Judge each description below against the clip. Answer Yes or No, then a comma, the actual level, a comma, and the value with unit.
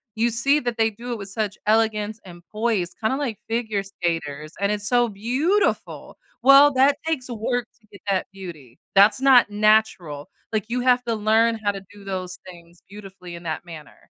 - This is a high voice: Yes, high, 215 Hz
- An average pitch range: Yes, average, 3.9 semitones